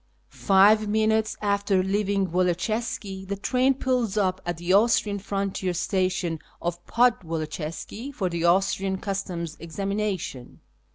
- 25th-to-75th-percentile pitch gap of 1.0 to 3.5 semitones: Yes, average, 3.0 semitones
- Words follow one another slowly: Yes, slow, 115 wpm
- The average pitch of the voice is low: No, high, 195 Hz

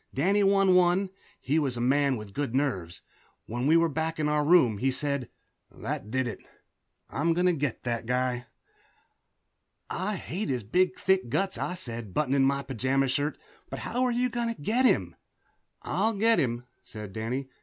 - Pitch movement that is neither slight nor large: No, wide, 6.6 semitones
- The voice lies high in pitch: No, medium, 145 Hz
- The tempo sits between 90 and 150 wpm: No, average, 180 wpm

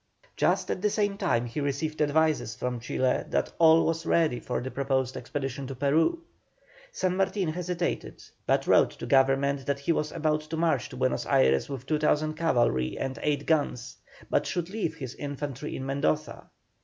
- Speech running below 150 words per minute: No, average, 175 wpm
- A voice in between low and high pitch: Yes, medium, 145 Hz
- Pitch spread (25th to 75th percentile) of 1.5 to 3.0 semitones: No, average, 3.5 semitones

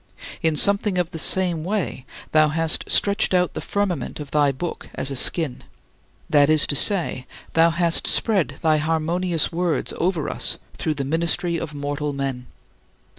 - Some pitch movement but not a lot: Yes, average, 3.2 semitones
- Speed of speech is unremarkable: Yes, average, 165 wpm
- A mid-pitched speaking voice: Yes, medium, 160 Hz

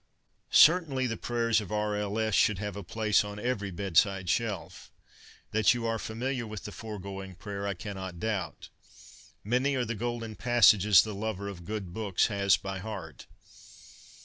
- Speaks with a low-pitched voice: Yes, low, 105 Hz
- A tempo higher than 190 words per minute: No, average, 170 wpm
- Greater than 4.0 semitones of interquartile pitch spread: No, narrow, 2.6 semitones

